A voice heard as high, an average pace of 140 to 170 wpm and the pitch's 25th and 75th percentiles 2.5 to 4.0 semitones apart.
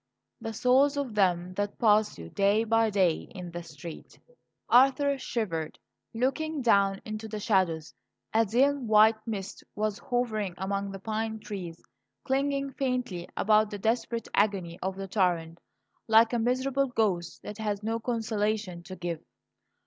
Yes: high, 215 Hz; average, 150 wpm; average, 3.6 semitones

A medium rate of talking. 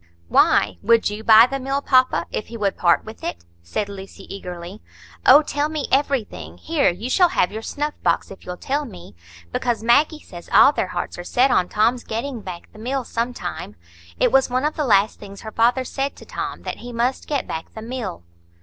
No: fast, 215 wpm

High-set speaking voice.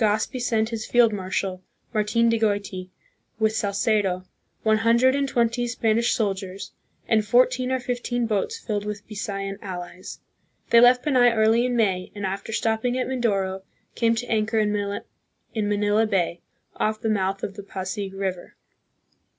Yes: high, 215 Hz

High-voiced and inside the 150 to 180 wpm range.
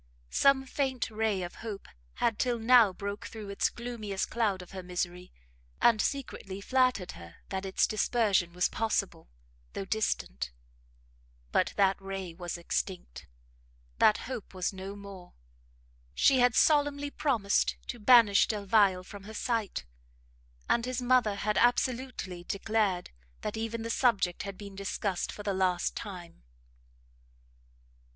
No: high, 205 Hz; slow, 135 wpm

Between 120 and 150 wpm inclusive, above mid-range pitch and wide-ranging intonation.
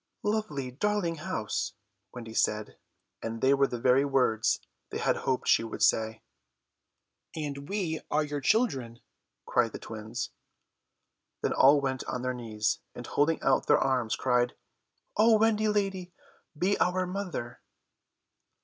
No: average, 140 wpm; low, 135 Hz; wide, 7.4 semitones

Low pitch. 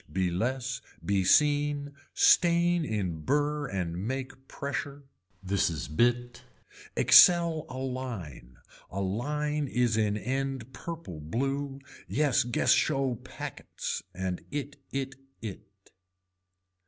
Yes: low, 130 Hz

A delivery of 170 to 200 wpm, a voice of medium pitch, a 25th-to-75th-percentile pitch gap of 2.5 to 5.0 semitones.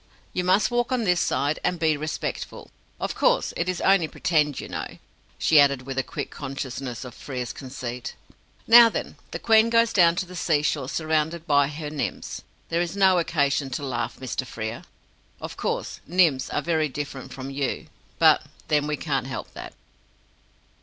Yes: average, 175 wpm; medium, 150 Hz; average, 4.5 semitones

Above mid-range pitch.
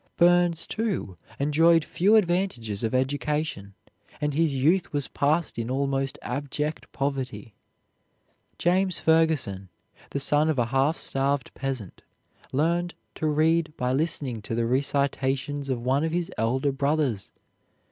No: medium, 145 Hz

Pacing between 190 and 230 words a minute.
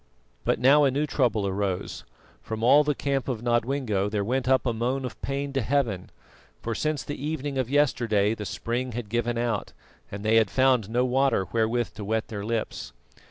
Yes: average, 195 wpm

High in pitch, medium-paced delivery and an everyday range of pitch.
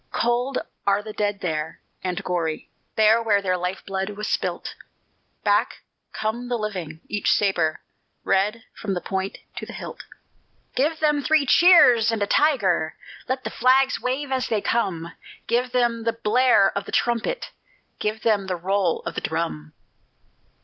Yes: high, 215 Hz; average, 160 wpm; average, 4.4 semitones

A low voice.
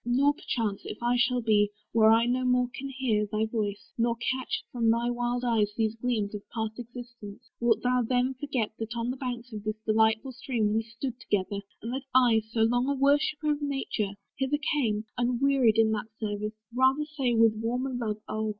No: high, 235 Hz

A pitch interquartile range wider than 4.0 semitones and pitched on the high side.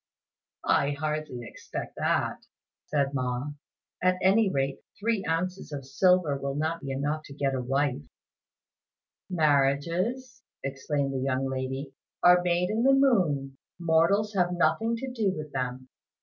No: average, 5.1 semitones; medium, 150 Hz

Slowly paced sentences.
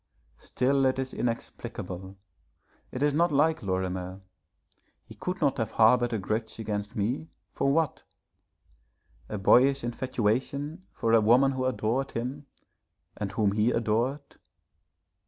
Yes: slow, 130 wpm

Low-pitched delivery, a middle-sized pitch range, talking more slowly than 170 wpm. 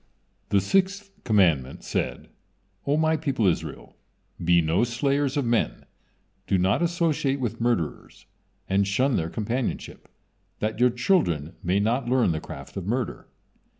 No: low, 120 Hz; wide, 6.3 semitones; average, 140 wpm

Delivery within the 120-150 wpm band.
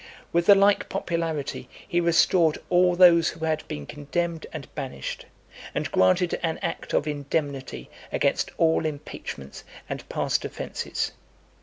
Yes: slow, 135 wpm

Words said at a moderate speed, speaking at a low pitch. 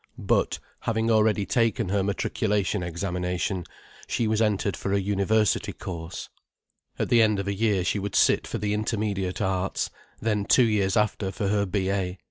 Yes: average, 165 wpm; low, 100 Hz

